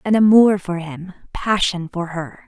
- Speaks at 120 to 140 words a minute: No, average, 170 wpm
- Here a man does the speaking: No, female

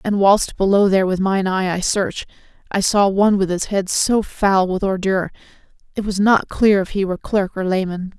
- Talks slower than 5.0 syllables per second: No, 5.2 syllables/s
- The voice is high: Yes, high, 195 Hz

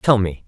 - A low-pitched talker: Yes, low, 105 Hz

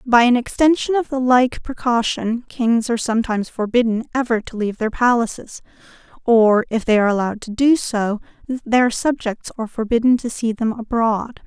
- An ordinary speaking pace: Yes, average, 165 wpm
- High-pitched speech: Yes, high, 235 Hz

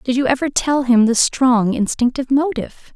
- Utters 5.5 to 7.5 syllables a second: No, 5.3 syllables/s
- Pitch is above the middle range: Yes, very high, 255 Hz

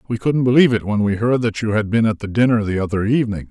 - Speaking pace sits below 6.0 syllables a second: No, 7.0 syllables/s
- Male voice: Yes, male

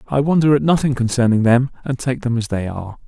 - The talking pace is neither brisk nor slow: No, fast, 235 wpm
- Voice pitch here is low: Yes, low, 125 Hz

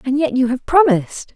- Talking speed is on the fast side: Yes, fast, 220 wpm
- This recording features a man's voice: No, female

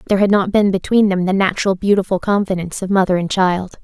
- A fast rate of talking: Yes, fast, 220 wpm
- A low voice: No, high, 190 Hz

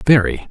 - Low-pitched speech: Yes, low, 105 Hz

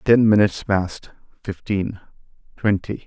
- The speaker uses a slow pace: Yes, slow, 100 wpm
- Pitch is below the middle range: Yes, low, 100 Hz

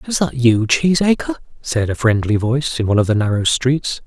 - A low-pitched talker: Yes, low, 125 Hz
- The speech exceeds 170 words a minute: Yes, fast, 205 wpm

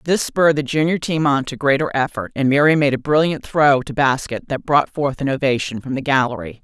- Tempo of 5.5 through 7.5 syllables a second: Yes, 5.6 syllables/s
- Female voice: Yes, female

